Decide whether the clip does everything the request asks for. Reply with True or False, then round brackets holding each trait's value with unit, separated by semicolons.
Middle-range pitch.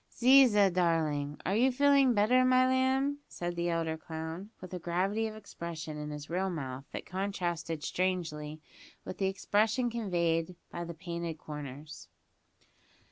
True (175 Hz)